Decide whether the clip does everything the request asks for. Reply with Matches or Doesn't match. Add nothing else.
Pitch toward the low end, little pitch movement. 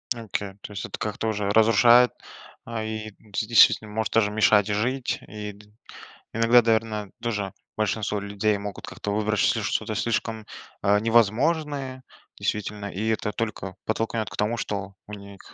Matches